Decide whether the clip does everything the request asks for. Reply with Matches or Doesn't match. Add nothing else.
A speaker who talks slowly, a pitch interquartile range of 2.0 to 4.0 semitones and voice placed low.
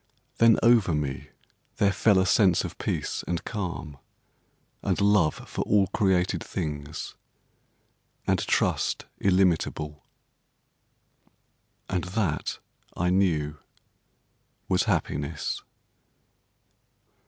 Doesn't match